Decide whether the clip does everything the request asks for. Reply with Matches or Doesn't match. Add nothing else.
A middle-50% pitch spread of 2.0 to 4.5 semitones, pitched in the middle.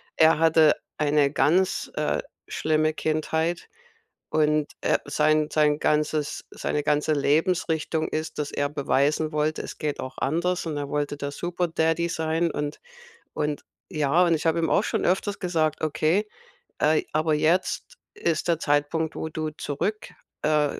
Doesn't match